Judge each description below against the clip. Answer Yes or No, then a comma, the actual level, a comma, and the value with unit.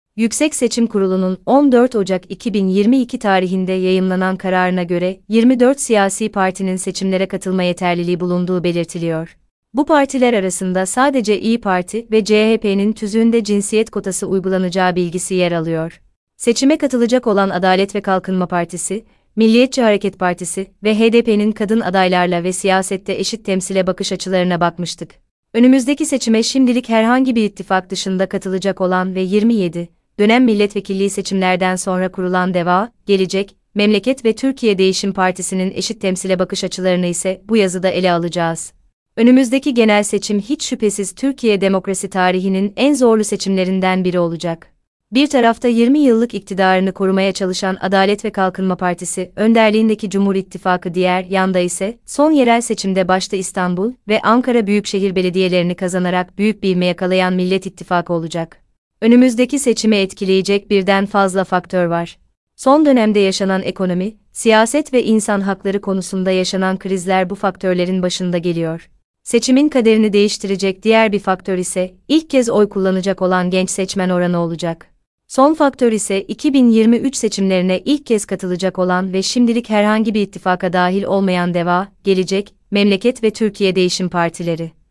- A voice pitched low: No, high, 195 Hz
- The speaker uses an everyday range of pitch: Yes, average, 3.0 semitones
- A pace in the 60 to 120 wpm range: No, average, 135 wpm